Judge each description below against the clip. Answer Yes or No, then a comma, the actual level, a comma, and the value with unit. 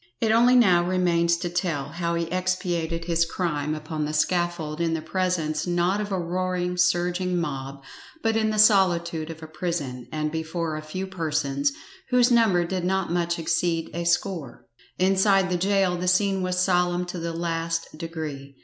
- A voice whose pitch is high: No, medium, 175 Hz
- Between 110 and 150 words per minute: No, average, 175 wpm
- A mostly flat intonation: Yes, narrow, 2.1 semitones